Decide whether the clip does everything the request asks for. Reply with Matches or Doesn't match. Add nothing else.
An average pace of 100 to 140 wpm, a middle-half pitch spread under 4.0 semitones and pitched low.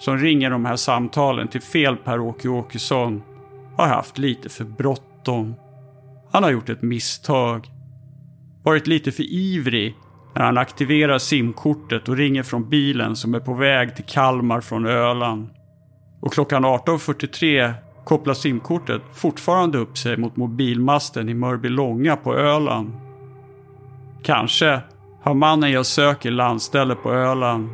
Matches